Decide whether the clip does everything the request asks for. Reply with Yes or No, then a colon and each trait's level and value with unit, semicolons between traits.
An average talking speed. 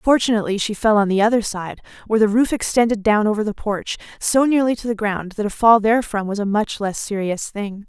No: fast, 230 wpm